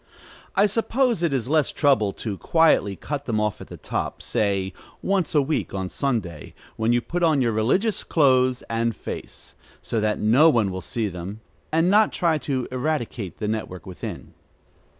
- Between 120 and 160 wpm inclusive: No, average, 175 wpm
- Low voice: Yes, low, 125 Hz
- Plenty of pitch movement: Yes, wide, 6.8 semitones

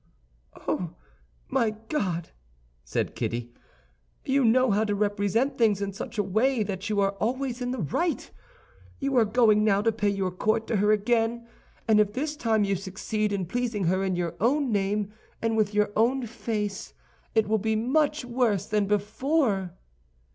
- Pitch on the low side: No, high, 215 Hz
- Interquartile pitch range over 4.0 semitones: No, average, 3.2 semitones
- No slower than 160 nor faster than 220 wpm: Yes, average, 170 wpm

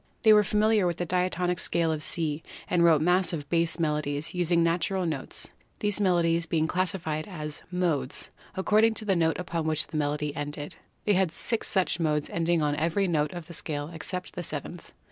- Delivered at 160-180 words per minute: No, average, 190 wpm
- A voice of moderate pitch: Yes, medium, 170 Hz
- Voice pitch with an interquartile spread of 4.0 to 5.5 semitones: No, average, 2.8 semitones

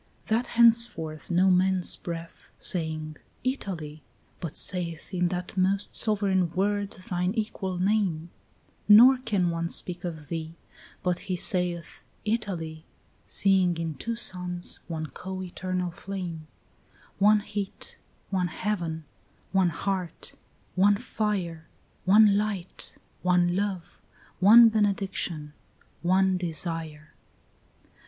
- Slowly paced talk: Yes, slow, 110 wpm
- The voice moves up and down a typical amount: Yes, average, 3.1 semitones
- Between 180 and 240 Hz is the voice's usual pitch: Yes, medium, 185 Hz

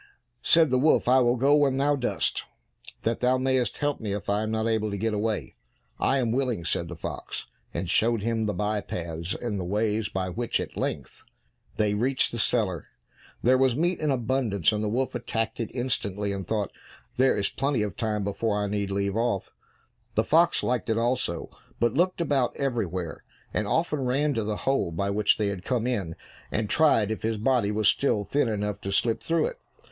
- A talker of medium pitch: No, low, 115 Hz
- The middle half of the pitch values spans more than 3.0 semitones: Yes, average, 4.1 semitones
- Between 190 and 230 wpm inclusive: Yes, fast, 205 wpm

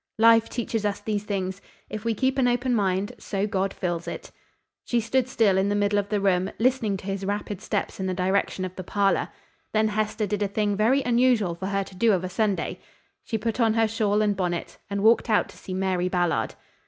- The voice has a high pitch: Yes, high, 205 Hz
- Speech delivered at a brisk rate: Yes, fast, 225 wpm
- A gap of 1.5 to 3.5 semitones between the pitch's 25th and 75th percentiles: Yes, average, 2.7 semitones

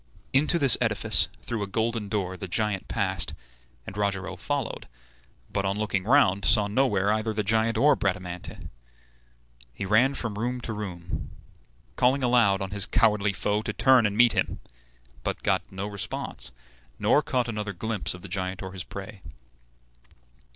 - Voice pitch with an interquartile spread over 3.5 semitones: No, average, 2.9 semitones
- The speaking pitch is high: No, low, 105 Hz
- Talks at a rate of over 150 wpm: Yes, average, 160 wpm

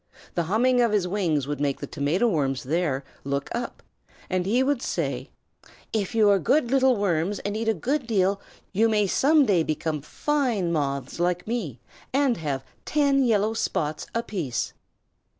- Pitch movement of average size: No, wide, 7.1 semitones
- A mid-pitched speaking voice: No, high, 200 Hz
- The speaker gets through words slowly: No, average, 170 wpm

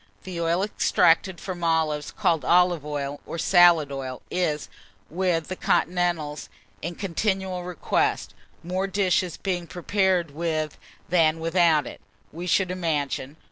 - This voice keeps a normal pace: No, slow, 130 wpm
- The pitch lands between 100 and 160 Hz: No, medium, 170 Hz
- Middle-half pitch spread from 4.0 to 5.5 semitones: No, average, 2.7 semitones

